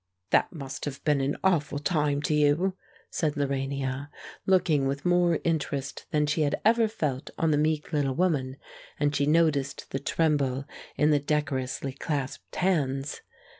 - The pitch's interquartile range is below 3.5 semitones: Yes, narrow, 2.5 semitones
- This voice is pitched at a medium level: Yes, medium, 145 Hz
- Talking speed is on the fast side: No, average, 155 wpm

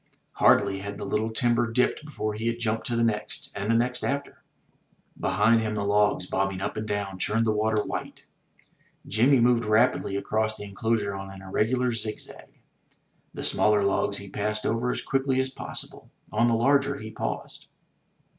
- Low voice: Yes, low, 110 Hz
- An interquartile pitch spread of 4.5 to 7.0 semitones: No, narrow, 2.5 semitones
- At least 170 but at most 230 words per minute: Yes, average, 180 wpm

